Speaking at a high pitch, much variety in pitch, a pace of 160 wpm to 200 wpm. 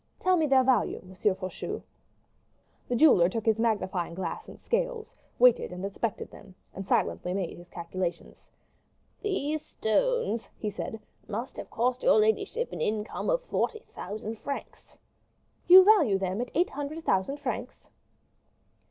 No: high, 225 Hz; wide, 7.7 semitones; average, 145 wpm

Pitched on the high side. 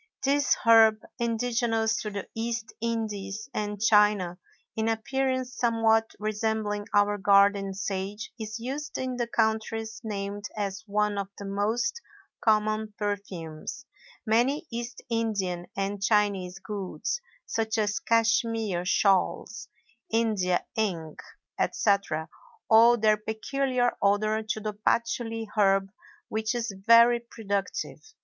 Yes: high, 215 Hz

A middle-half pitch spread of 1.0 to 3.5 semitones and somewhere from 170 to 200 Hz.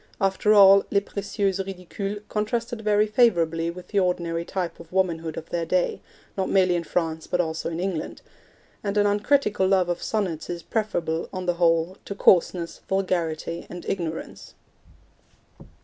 Yes: average, 3.1 semitones; medium, 185 Hz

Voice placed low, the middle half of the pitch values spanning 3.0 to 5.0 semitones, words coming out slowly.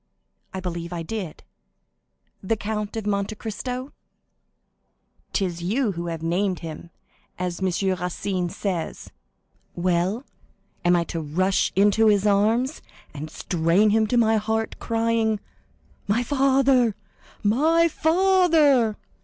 No: high, 205 Hz; average, 4.4 semitones; slow, 120 wpm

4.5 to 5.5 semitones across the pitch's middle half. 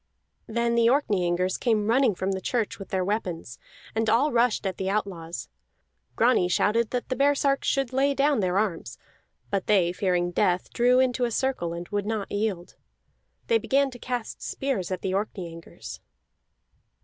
Yes: average, 5.2 semitones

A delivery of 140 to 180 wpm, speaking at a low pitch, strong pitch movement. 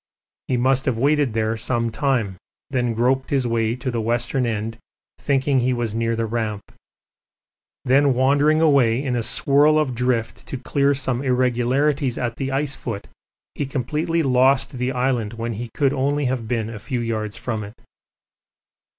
No: average, 170 wpm; low, 125 Hz; average, 3.0 semitones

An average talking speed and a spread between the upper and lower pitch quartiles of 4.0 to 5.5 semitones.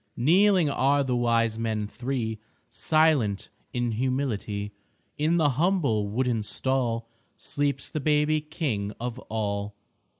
No: slow, 120 wpm; average, 5.0 semitones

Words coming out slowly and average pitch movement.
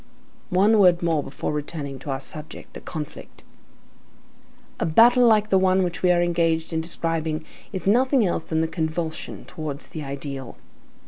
No: average, 165 wpm; average, 3.3 semitones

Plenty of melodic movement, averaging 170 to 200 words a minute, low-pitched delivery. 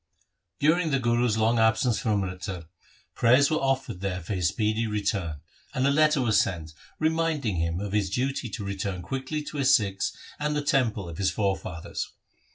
Yes: wide, 5.8 semitones; average, 175 wpm; low, 110 Hz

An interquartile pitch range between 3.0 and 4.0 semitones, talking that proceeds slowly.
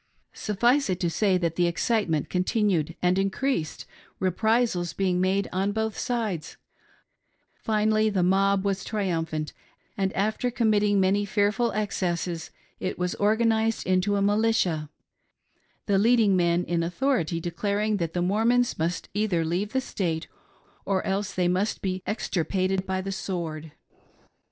No: average, 3.3 semitones; average, 145 wpm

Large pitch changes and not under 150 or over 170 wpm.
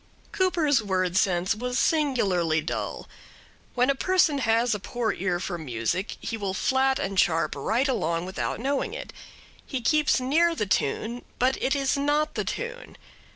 Yes: wide, 7.1 semitones; average, 160 wpm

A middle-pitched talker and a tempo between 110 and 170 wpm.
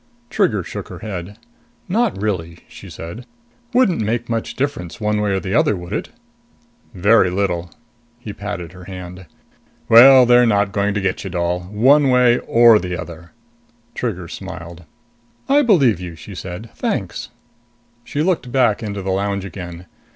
No: low, 100 Hz; average, 160 wpm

